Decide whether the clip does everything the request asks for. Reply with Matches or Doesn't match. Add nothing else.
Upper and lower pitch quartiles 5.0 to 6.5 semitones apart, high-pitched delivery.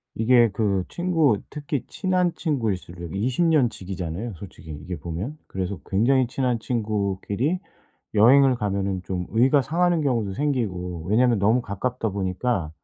Doesn't match